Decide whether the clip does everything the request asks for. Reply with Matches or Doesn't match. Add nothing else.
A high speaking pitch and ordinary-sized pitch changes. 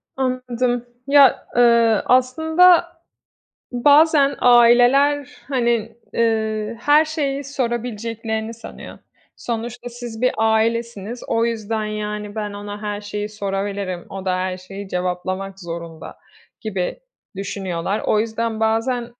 Matches